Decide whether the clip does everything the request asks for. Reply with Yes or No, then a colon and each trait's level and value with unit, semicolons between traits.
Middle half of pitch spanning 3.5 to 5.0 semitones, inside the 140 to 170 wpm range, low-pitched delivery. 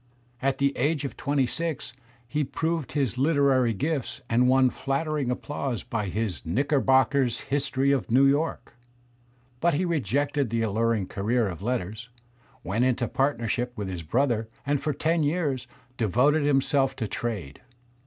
Yes: average, 3.8 semitones; average, 145 wpm; low, 130 Hz